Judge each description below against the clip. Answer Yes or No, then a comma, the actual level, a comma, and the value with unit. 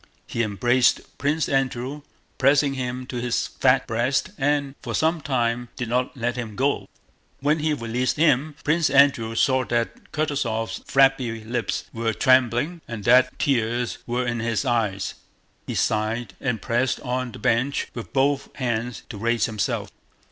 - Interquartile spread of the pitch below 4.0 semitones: Yes, average, 2.8 semitones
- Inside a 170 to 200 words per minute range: No, average, 155 wpm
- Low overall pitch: Yes, low, 125 Hz